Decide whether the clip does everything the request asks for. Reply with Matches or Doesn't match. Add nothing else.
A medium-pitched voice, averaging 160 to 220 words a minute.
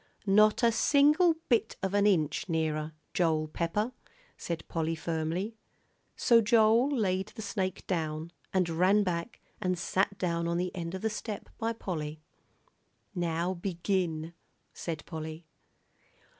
Doesn't match